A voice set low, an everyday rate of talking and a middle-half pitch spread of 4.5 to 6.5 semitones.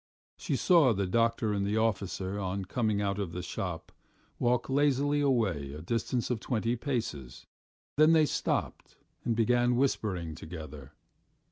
Yes: low, 110 Hz; average, 145 wpm; average, 5.1 semitones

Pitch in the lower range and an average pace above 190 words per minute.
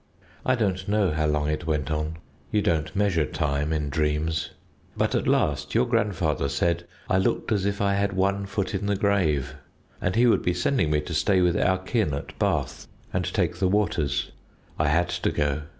Yes: very low, 90 Hz; average, 200 wpm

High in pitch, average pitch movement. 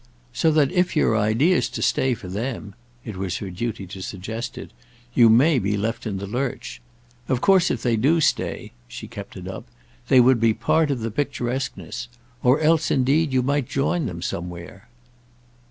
No: low, 120 Hz; average, 4.7 semitones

